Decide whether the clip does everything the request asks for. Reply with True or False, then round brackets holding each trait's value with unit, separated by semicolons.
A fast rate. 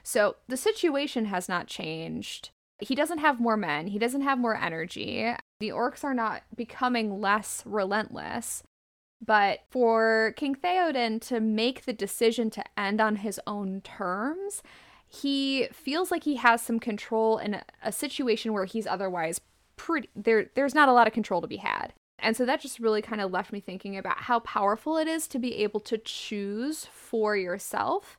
False (180 wpm)